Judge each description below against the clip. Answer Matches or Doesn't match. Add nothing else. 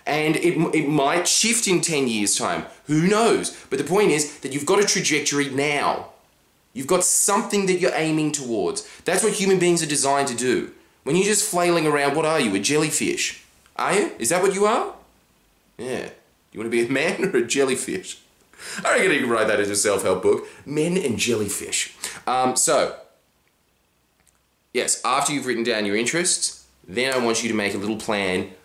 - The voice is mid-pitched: Matches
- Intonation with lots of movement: Matches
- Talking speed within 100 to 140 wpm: Doesn't match